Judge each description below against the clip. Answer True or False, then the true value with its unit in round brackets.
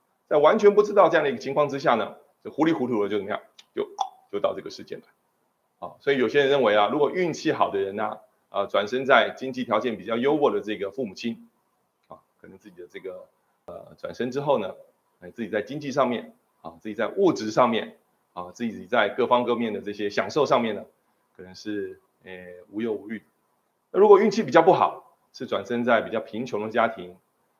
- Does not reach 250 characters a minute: False (310 characters per minute)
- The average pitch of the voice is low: True (120 Hz)